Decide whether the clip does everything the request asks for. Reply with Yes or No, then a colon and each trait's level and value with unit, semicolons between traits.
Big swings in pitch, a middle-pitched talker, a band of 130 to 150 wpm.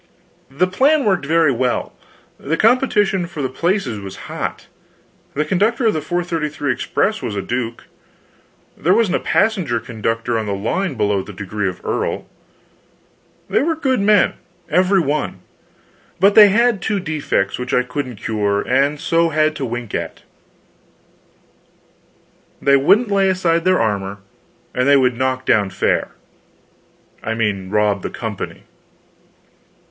Yes: wide, 8.9 semitones; medium, 145 Hz; average, 145 wpm